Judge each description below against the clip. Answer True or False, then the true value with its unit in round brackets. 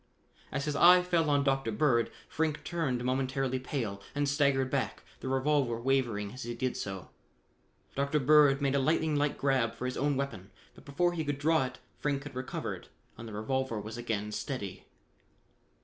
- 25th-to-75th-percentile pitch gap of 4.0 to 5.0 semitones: False (3.4 semitones)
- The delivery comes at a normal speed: True (180 wpm)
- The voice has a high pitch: False (135 Hz)